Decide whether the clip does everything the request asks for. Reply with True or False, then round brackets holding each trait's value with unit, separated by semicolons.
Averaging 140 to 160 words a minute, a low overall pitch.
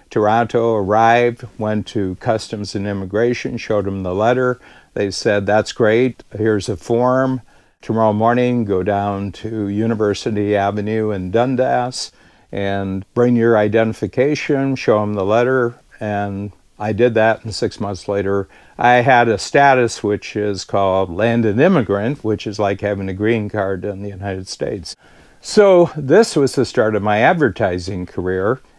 True (150 wpm; 110 Hz)